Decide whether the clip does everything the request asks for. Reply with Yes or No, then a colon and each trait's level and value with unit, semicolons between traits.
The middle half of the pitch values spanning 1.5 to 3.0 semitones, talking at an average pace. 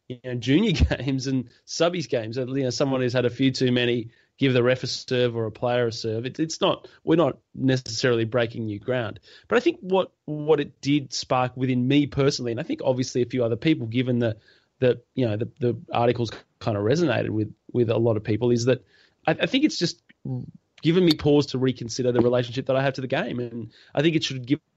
No: narrow, 2.6 semitones; fast, 235 wpm